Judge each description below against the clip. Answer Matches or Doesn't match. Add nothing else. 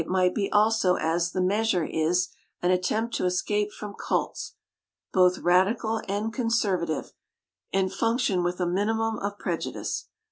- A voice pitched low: Doesn't match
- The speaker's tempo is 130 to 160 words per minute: Matches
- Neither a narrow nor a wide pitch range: Matches